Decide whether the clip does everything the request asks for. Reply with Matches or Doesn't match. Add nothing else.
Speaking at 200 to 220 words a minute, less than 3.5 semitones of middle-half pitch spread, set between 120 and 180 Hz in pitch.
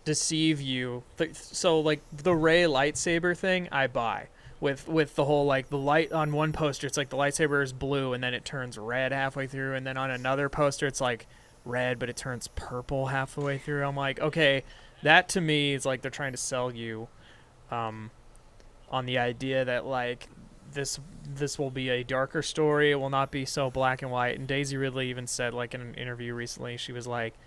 Matches